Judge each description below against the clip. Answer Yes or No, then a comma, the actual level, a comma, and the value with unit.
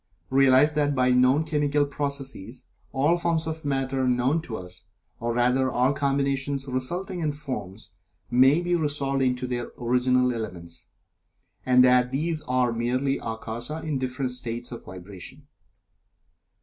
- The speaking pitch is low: Yes, low, 130 Hz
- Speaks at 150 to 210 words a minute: No, average, 140 wpm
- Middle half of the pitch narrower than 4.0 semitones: Yes, narrow, 2.6 semitones